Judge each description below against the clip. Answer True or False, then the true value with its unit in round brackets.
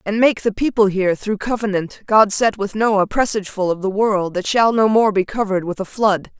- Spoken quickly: True (225 wpm)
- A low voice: False (205 Hz)